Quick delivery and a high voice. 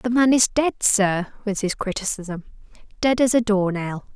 No: average, 190 wpm; high, 210 Hz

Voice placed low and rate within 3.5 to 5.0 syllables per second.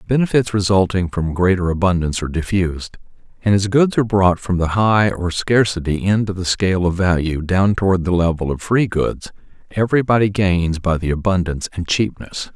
No: very low, 95 Hz; 5.6 syllables/s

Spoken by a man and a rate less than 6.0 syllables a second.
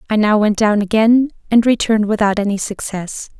No: female; 5.5 syllables/s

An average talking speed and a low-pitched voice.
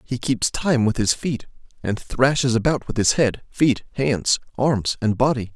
Yes: average, 185 wpm; low, 125 Hz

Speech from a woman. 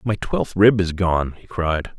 No: male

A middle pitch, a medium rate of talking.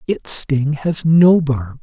Yes: medium, 150 Hz; average, 165 wpm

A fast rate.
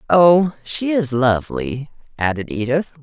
No: slow, 120 wpm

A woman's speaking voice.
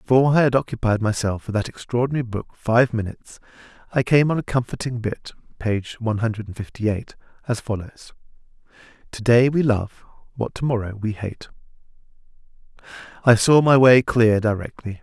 No: male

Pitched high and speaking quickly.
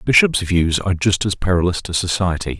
No: very low, 95 Hz; fast, 210 wpm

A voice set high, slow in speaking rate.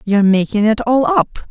No: high, 225 Hz; average, 200 wpm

